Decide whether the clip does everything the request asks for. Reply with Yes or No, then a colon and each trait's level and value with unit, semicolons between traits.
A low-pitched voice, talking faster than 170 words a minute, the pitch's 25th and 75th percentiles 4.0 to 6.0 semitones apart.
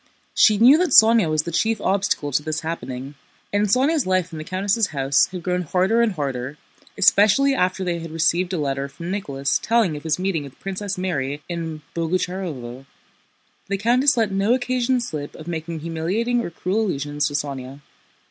No: medium, 180 Hz; average, 180 wpm; wide, 5.5 semitones